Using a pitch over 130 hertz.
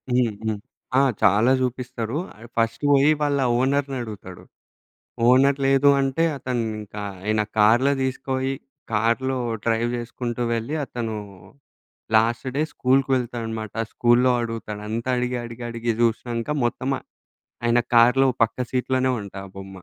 No: low, 120 Hz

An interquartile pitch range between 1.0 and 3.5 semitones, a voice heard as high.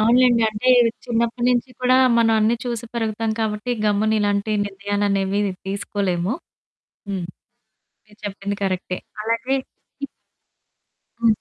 Yes: narrow, 2.6 semitones; high, 215 Hz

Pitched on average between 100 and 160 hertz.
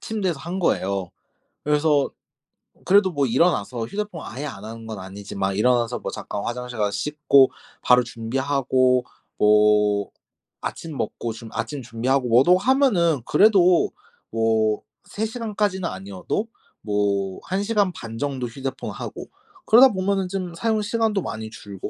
Yes: low, 135 Hz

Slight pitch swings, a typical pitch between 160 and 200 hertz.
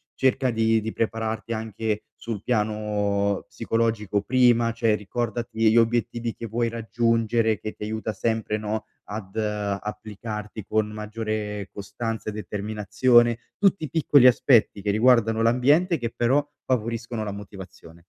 No: narrow, 1.8 semitones; low, 110 Hz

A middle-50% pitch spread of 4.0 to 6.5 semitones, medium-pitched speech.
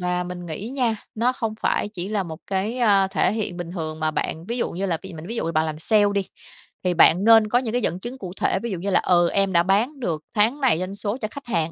No: average, 4.5 semitones; high, 195 Hz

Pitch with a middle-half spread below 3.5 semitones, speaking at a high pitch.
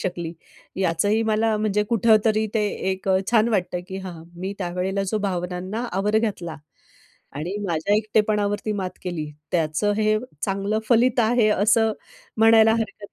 Yes: average, 3.1 semitones; high, 205 Hz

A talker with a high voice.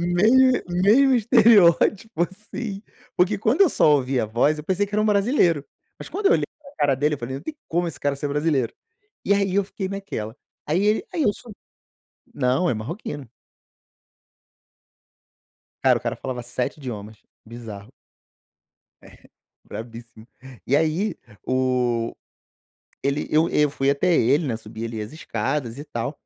No: medium, 150 Hz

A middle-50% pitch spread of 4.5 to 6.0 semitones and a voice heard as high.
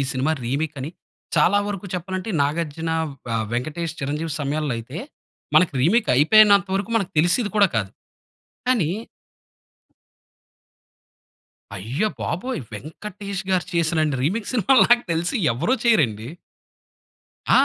No: wide, 5.6 semitones; medium, 165 Hz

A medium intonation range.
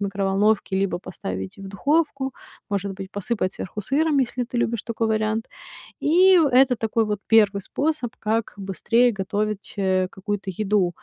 Yes: average, 3.8 semitones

